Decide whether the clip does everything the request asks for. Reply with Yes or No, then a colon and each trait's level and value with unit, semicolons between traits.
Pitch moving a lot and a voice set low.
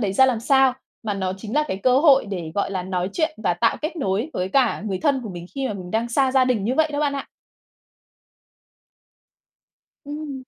No: wide, 6.1 semitones; high, 240 Hz